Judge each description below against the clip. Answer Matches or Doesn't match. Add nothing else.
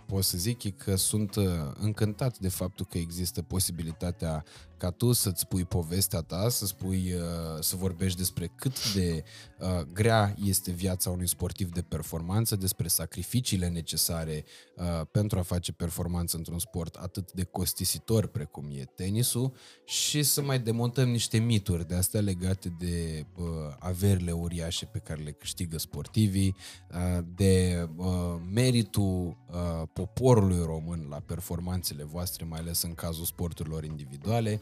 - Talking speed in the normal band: Matches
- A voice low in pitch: Matches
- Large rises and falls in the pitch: Doesn't match